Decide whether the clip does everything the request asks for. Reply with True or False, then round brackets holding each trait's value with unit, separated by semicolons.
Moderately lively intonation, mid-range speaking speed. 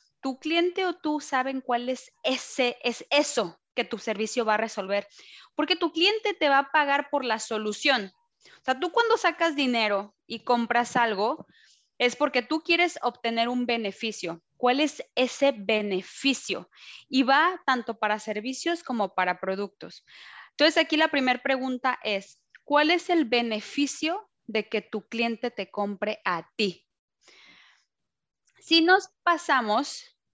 False (5.9 semitones; 150 wpm)